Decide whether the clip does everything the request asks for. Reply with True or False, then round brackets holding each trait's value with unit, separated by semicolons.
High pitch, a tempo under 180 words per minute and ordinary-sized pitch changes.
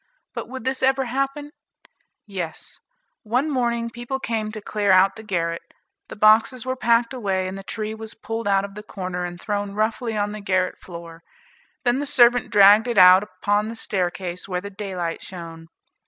False (210 Hz; 185 wpm; 4.0 semitones)